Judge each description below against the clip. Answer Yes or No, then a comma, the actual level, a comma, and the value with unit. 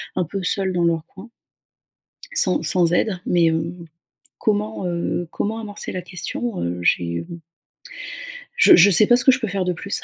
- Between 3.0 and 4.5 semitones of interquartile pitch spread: Yes, average, 3.4 semitones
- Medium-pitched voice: Yes, medium, 180 Hz